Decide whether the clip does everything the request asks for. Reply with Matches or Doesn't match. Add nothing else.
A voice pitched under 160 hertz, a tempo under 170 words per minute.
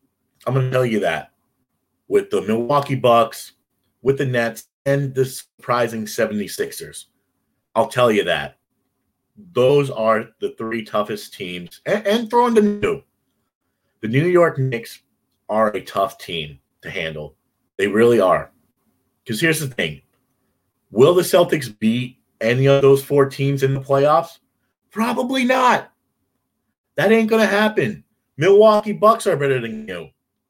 Matches